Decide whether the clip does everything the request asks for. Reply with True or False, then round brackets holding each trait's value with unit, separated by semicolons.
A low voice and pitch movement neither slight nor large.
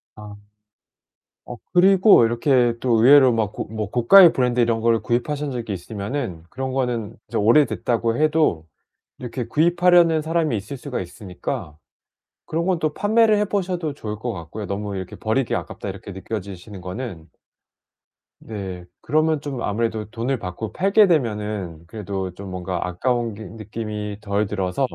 False (115 Hz; 6.1 semitones)